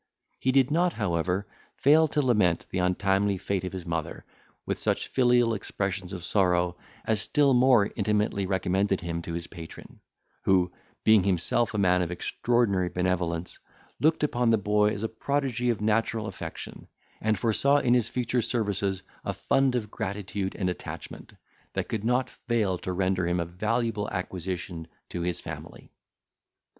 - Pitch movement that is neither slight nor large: Yes, average, 4.6 semitones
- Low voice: Yes, low, 100 Hz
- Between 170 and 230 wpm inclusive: No, average, 160 wpm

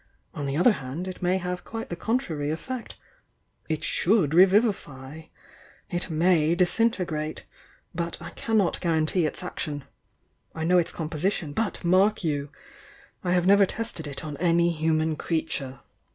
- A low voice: No, medium, 170 Hz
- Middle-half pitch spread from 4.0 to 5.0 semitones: No, average, 3.2 semitones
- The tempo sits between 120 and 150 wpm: No, average, 165 wpm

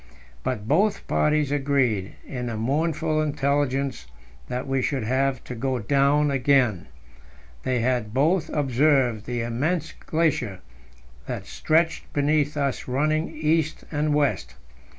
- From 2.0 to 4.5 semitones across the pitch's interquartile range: Yes, average, 3.4 semitones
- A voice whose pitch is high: No, medium, 140 Hz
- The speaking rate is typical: No, slow, 125 wpm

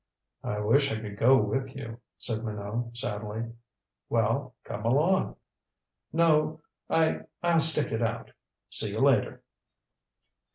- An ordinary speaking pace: No, slow, 130 wpm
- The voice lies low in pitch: Yes, low, 120 Hz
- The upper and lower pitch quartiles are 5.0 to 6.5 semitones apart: Yes, wide, 5.6 semitones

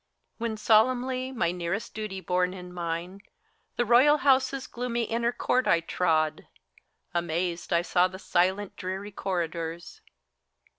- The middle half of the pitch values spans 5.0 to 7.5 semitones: Yes, wide, 5.4 semitones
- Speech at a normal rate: No, slow, 130 wpm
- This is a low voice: No, high, 190 Hz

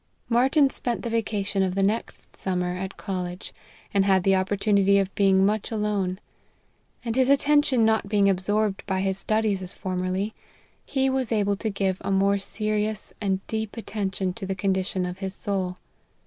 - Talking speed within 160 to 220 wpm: Yes, average, 175 wpm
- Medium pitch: No, high, 200 Hz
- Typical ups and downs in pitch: No, narrow, 2.3 semitones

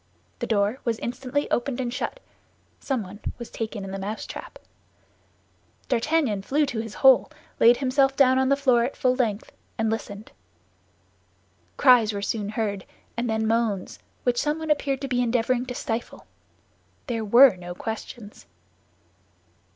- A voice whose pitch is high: Yes, high, 235 Hz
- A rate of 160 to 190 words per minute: No, average, 145 wpm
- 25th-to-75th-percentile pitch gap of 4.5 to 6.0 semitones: No, average, 3.2 semitones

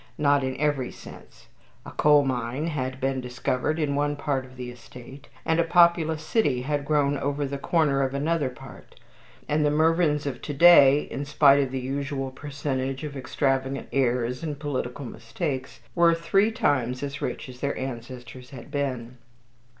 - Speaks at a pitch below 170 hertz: Yes, medium, 140 Hz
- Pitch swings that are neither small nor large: No, narrow, 2.3 semitones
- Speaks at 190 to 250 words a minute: No, average, 170 wpm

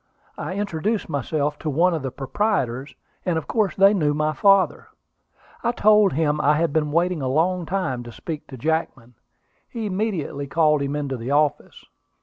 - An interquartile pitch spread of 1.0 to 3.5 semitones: No, average, 4.8 semitones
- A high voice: No, medium, 155 Hz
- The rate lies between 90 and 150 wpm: No, average, 175 wpm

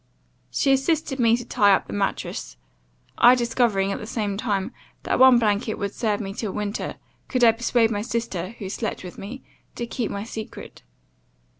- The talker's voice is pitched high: Yes, high, 225 Hz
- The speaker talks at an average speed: Yes, average, 180 wpm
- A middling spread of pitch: Yes, average, 3.1 semitones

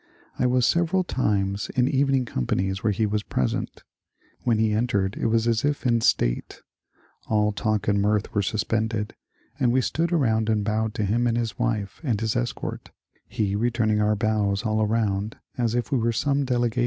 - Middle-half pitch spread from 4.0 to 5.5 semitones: No, narrow, 2.6 semitones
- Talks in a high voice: No, low, 110 Hz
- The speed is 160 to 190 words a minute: Yes, average, 185 wpm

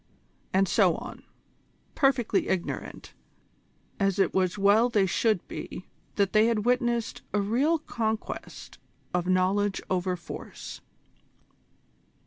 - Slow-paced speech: Yes, slow, 110 wpm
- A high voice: Yes, high, 205 Hz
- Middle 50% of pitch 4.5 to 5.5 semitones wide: No, average, 3.6 semitones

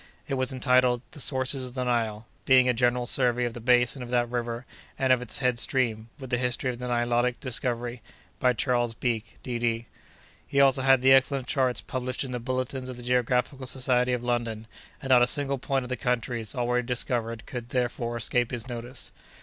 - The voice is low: Yes, low, 125 Hz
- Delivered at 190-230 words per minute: Yes, average, 200 wpm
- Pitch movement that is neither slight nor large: No, narrow, 1.2 semitones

